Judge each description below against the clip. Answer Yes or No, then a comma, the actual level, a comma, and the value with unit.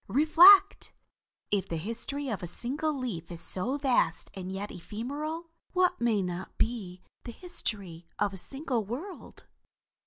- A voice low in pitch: No, high, 235 Hz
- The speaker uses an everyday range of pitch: No, wide, 7.6 semitones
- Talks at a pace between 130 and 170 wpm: Yes, average, 145 wpm